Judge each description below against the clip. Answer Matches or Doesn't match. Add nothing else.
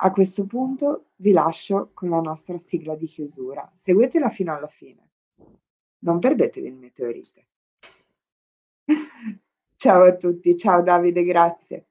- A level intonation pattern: Doesn't match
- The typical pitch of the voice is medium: Matches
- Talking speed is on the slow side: Doesn't match